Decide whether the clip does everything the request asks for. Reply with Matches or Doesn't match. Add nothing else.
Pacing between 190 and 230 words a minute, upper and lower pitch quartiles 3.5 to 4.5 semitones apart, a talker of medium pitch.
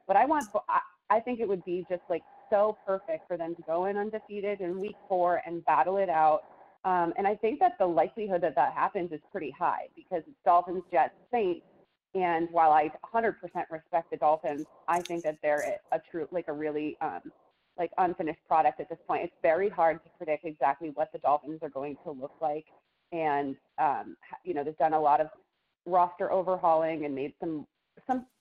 Matches